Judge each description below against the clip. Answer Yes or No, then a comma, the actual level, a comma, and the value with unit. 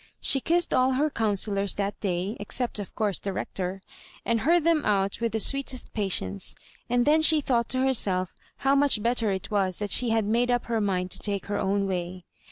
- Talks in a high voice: Yes, high, 215 Hz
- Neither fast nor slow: No, fast, 210 wpm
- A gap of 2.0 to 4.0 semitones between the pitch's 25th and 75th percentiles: No, average, 4.7 semitones